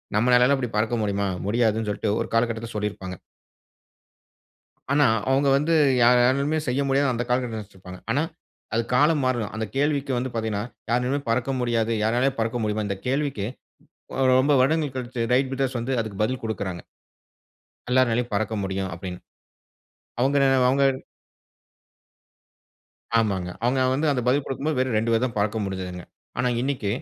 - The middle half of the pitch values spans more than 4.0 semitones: No, average, 3.7 semitones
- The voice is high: No, low, 120 Hz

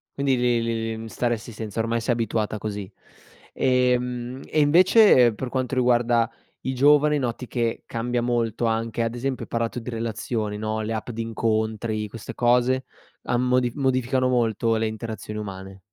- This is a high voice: No, low, 115 Hz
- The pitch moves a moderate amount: No, narrow, 2.1 semitones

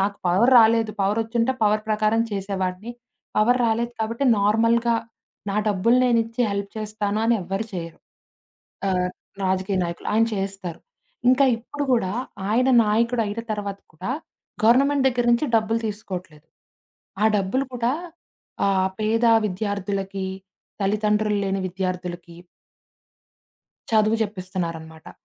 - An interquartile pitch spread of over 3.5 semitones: No, average, 3.1 semitones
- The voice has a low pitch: No, high, 210 Hz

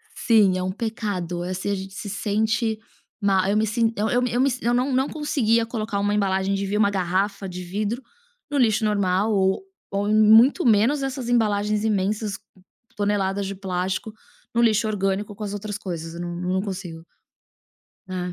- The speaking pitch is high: Yes, high, 205 Hz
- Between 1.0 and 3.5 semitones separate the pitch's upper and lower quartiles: Yes, narrow, 2.6 semitones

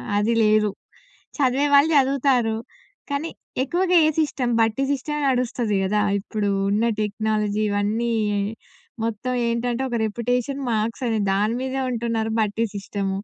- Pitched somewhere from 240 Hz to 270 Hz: No, high, 230 Hz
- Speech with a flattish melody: No, average, 3.6 semitones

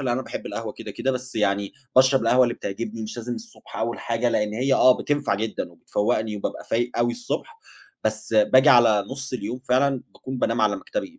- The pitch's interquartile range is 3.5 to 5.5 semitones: No, average, 3.1 semitones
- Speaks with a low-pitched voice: Yes, low, 120 Hz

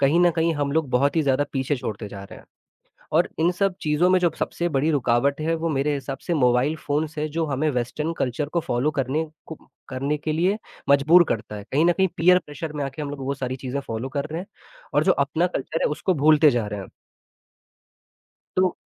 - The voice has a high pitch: No, medium, 145 Hz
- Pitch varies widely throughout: No, average, 3.5 semitones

